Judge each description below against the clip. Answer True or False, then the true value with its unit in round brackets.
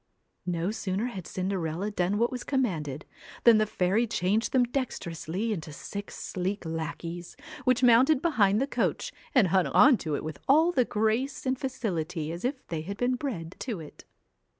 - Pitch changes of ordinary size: False (6.4 semitones)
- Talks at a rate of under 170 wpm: False (175 wpm)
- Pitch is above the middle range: True (205 Hz)